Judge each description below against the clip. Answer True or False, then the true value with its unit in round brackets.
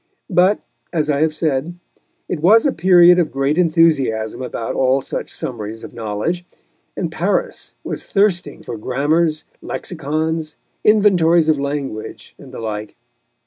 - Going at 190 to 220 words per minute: False (140 wpm)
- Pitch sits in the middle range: True (155 Hz)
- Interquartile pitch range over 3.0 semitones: True (4.8 semitones)